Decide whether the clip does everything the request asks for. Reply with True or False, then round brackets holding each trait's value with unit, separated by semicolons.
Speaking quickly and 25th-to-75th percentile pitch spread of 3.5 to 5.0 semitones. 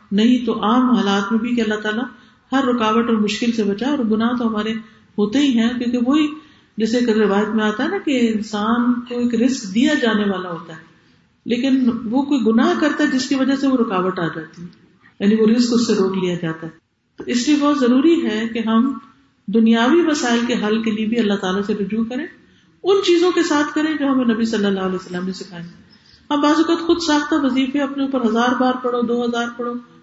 True (225 wpm; 3.9 semitones)